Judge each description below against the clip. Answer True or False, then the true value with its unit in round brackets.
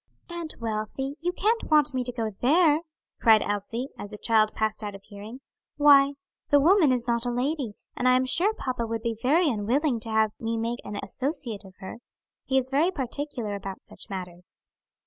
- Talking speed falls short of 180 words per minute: False (195 wpm)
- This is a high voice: True (245 Hz)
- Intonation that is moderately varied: True (4.9 semitones)